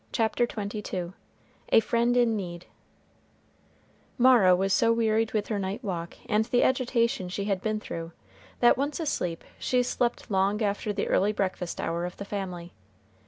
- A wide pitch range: No, average, 3.9 semitones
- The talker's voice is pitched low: No, high, 210 Hz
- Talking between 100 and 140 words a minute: No, average, 160 wpm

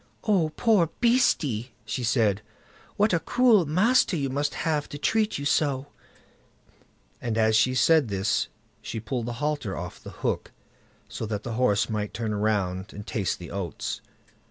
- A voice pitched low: Yes, low, 125 Hz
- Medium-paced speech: Yes, average, 160 wpm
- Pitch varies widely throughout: Yes, wide, 6.8 semitones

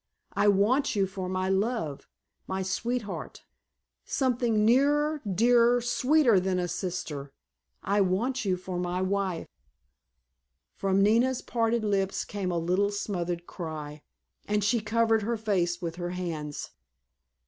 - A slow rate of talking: Yes, slow, 125 wpm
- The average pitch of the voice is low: No, high, 200 Hz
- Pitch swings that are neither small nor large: Yes, average, 4.2 semitones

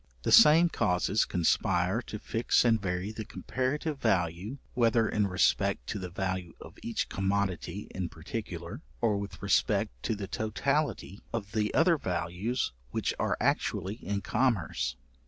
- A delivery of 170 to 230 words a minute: No, average, 145 wpm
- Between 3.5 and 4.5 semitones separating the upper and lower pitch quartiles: Yes, average, 4.1 semitones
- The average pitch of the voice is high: No, low, 100 Hz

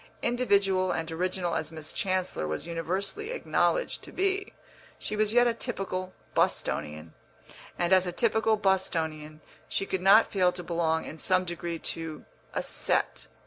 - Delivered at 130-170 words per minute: Yes, average, 150 wpm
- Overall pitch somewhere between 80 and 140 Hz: No, medium, 185 Hz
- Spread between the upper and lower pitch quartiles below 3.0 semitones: No, average, 3.9 semitones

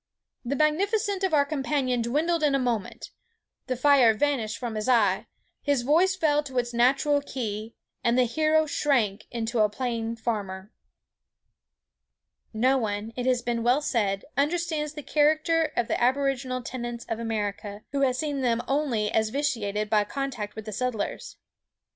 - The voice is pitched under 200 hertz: No, very high, 250 Hz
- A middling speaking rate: Yes, average, 160 wpm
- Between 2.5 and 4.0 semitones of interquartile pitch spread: No, average, 4.5 semitones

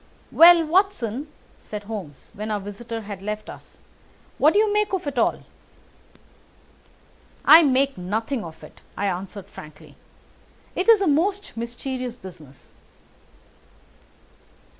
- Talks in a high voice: Yes, high, 230 Hz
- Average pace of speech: No, slow, 125 wpm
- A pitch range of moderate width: No, wide, 8.0 semitones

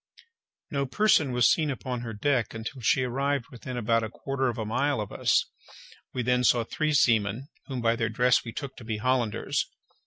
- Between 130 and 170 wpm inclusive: No, average, 195 wpm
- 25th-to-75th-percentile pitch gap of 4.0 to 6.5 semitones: No, average, 3.0 semitones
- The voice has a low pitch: Yes, low, 125 Hz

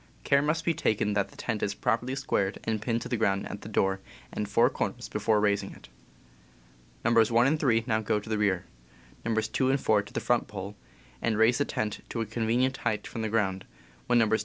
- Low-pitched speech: Yes, low, 110 Hz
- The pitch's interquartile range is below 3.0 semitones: Yes, narrow, 2.6 semitones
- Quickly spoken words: Yes, fast, 225 wpm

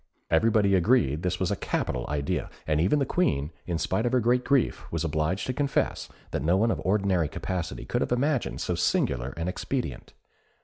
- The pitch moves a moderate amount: No, wide, 7.1 semitones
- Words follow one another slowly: No, average, 190 wpm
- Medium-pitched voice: No, very low, 95 Hz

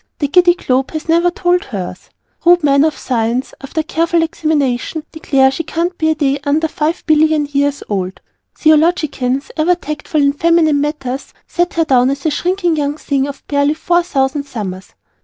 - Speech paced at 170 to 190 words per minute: Yes, average, 175 wpm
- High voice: Yes, very high, 300 Hz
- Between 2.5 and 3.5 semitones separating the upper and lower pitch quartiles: Yes, average, 3.2 semitones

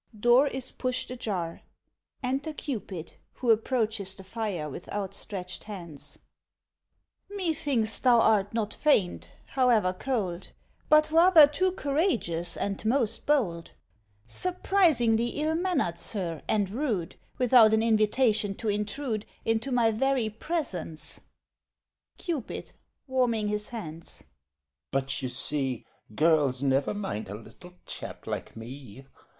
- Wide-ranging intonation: Yes, wide, 6.6 semitones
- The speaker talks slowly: Yes, slow, 120 wpm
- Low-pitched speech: No, high, 220 Hz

